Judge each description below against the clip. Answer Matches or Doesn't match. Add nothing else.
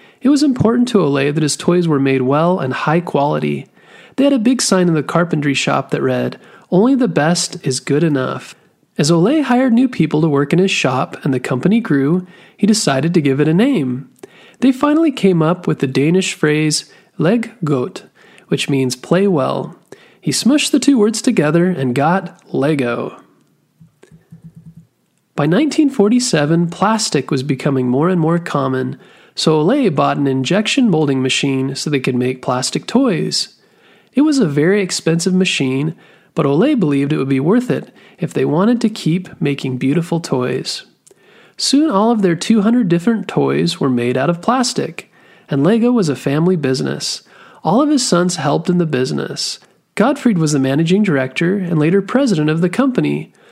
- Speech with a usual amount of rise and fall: Doesn't match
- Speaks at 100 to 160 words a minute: Doesn't match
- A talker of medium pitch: Matches